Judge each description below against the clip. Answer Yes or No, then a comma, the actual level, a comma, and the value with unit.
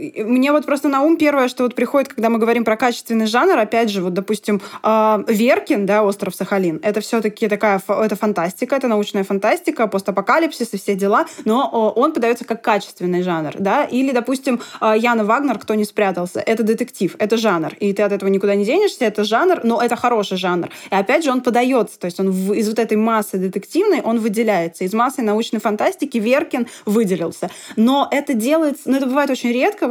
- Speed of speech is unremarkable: No, fast, 190 wpm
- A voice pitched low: No, high, 225 Hz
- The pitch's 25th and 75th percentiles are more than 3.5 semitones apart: Yes, average, 4.0 semitones